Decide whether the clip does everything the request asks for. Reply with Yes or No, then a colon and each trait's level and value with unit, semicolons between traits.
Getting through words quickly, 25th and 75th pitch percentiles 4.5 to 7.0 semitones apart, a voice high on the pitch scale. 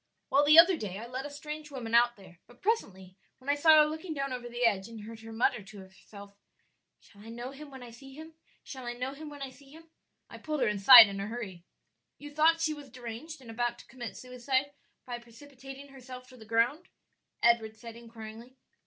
No: fast, 225 wpm; average, 4.0 semitones; very high, 250 Hz